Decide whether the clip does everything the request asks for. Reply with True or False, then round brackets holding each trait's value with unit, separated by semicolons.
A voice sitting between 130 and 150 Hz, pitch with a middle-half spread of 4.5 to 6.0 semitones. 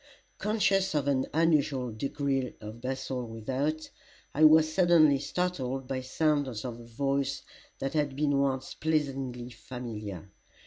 False (135 Hz; 3.4 semitones)